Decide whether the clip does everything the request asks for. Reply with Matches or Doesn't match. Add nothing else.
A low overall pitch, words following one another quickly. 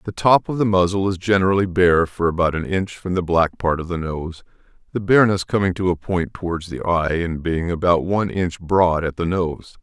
Matches